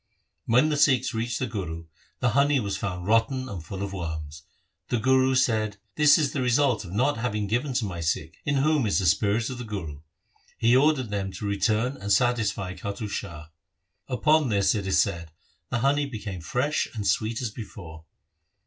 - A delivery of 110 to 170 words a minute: No, average, 190 wpm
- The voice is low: Yes, low, 110 Hz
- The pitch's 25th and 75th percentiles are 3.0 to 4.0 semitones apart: No, average, 5.0 semitones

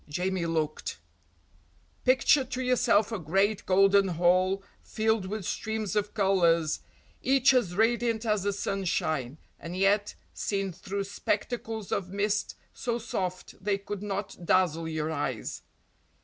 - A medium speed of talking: No, slow, 130 wpm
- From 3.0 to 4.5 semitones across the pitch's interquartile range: Yes, average, 3.3 semitones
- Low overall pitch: No, high, 195 Hz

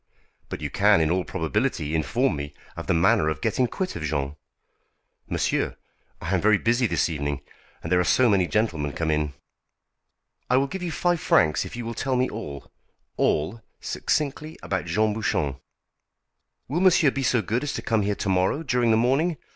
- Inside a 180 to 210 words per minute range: Yes, average, 185 wpm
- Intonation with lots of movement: Yes, wide, 8.4 semitones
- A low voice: Yes, low, 105 Hz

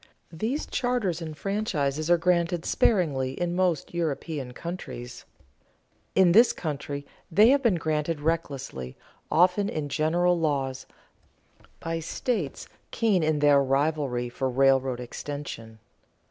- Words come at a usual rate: No, slow, 120 wpm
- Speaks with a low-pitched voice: No, medium, 155 Hz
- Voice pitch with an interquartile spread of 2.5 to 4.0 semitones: No, average, 4.4 semitones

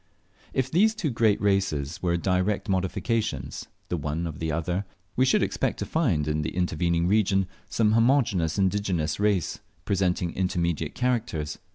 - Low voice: Yes, very low, 95 Hz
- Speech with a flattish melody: No, average, 4.4 semitones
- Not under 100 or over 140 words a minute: No, average, 150 wpm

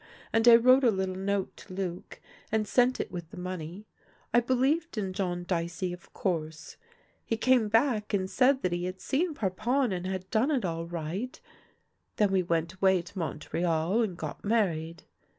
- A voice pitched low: No, high, 190 Hz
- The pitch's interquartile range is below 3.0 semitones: No, average, 4.7 semitones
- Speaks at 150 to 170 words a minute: No, average, 185 wpm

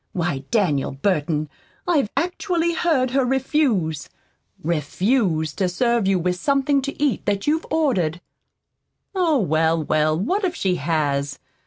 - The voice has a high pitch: Yes, high, 195 Hz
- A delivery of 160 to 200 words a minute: No, slow, 135 wpm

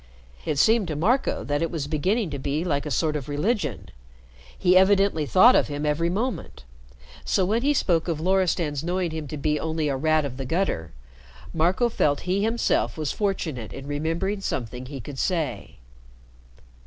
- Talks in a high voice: No, medium, 160 Hz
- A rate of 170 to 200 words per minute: Yes, average, 180 wpm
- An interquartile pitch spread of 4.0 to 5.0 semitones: Yes, average, 4.7 semitones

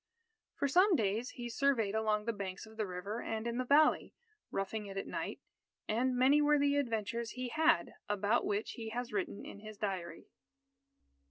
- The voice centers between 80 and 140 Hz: No, high, 225 Hz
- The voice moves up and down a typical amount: Yes, average, 3.7 semitones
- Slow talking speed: No, average, 180 wpm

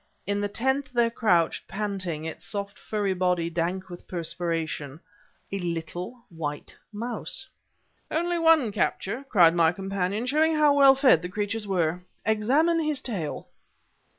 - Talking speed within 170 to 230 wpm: No, average, 140 wpm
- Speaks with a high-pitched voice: Yes, high, 200 Hz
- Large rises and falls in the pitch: Yes, wide, 6.3 semitones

